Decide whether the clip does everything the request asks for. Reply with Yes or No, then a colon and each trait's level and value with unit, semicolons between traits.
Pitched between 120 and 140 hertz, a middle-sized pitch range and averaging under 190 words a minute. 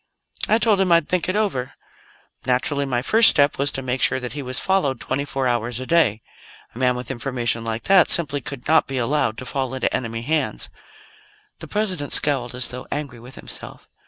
No: low, 135 Hz; average, 3.7 semitones; fast, 205 wpm